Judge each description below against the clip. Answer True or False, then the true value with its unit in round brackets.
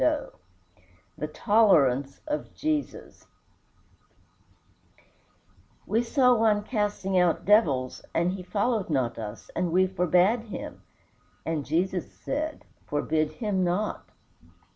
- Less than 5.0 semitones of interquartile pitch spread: False (5.6 semitones)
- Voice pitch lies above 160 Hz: True (185 Hz)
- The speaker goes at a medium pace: False (105 wpm)